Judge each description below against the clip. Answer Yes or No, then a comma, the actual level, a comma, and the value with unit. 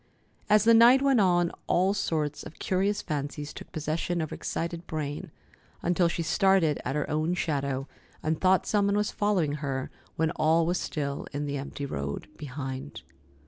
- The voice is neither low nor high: Yes, medium, 160 Hz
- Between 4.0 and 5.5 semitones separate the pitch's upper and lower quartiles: Yes, average, 4.4 semitones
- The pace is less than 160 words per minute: No, average, 175 wpm